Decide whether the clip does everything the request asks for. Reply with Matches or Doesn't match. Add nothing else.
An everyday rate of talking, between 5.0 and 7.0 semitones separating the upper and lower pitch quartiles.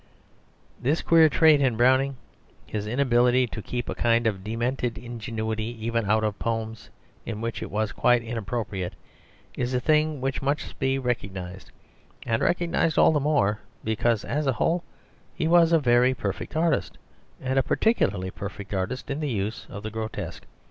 Doesn't match